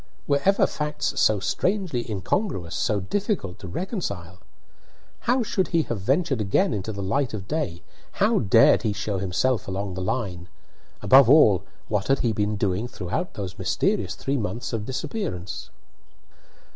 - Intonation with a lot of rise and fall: Yes, wide, 7.8 semitones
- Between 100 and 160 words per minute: Yes, average, 155 wpm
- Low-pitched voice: Yes, low, 110 Hz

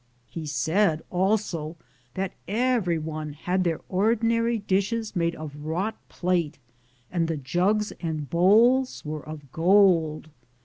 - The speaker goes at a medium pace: No, slow, 120 wpm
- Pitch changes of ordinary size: Yes, average, 4.9 semitones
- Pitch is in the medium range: Yes, medium, 175 Hz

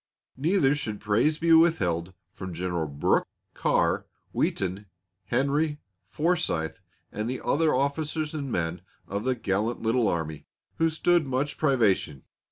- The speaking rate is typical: No, slow, 130 wpm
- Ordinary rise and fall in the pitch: No, wide, 8.4 semitones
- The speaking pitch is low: Yes, low, 125 Hz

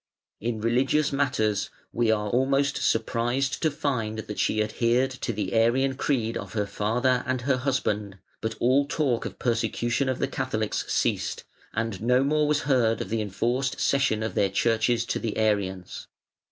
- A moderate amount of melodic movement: Yes, average, 3.3 semitones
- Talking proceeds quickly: No, average, 165 wpm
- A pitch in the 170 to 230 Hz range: No, low, 120 Hz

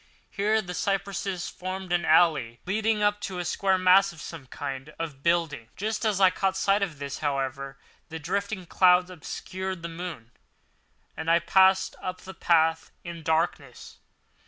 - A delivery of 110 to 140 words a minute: No, average, 160 wpm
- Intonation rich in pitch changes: No, average, 3.2 semitones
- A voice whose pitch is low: No, medium, 180 Hz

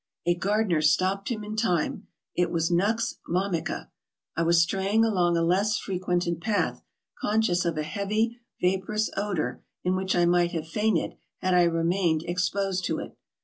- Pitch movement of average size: Yes, average, 3.0 semitones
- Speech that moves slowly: No, average, 160 wpm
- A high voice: No, medium, 180 Hz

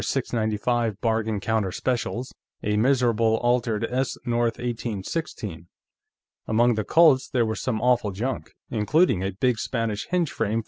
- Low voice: Yes, low, 115 Hz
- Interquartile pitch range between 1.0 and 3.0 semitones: Yes, average, 2.7 semitones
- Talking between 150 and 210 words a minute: No, slow, 135 wpm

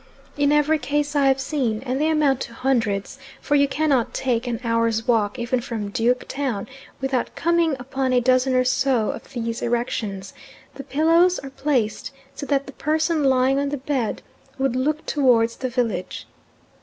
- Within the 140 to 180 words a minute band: Yes, average, 175 wpm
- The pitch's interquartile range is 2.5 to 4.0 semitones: Yes, average, 3.3 semitones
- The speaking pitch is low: No, very high, 260 Hz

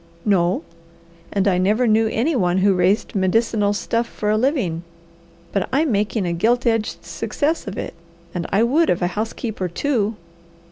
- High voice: Yes, high, 210 Hz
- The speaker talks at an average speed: Yes, average, 170 wpm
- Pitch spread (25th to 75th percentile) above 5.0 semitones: No, average, 3.8 semitones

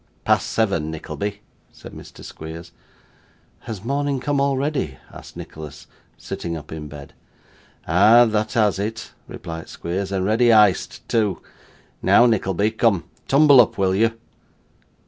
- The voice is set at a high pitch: No, low, 105 Hz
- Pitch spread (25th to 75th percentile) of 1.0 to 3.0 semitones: No, wide, 5.4 semitones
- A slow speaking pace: Yes, slow, 130 wpm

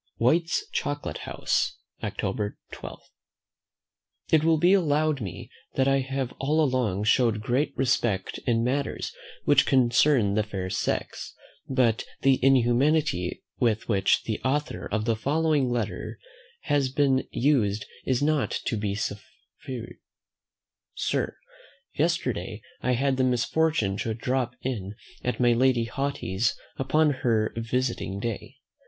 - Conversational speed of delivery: No, slow, 125 wpm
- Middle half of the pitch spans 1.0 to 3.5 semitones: No, average, 4.1 semitones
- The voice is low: Yes, low, 125 Hz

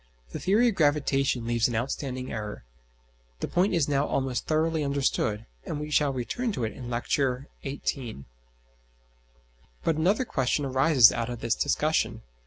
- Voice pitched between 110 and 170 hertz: Yes, low, 135 Hz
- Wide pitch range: No, average, 4.0 semitones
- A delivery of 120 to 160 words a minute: Yes, average, 155 wpm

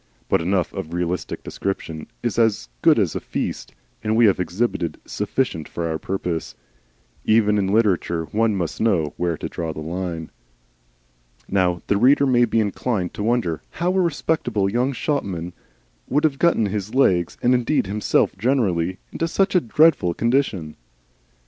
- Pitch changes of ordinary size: No, wide, 5.8 semitones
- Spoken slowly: No, average, 160 wpm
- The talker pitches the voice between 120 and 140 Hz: No, low, 100 Hz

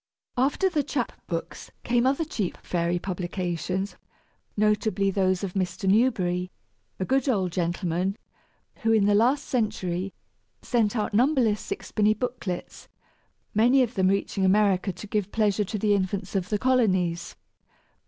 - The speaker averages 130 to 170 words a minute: Yes, average, 140 wpm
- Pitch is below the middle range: No, high, 205 Hz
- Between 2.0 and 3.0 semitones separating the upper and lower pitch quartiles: No, average, 3.7 semitones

